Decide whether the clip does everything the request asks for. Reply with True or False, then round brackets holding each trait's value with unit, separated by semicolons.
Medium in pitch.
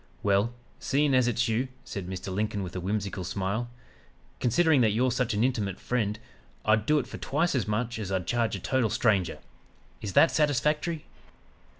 False (115 Hz)